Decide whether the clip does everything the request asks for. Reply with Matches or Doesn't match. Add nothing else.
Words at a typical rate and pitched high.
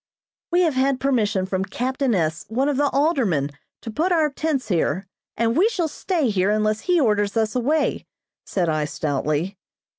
Matches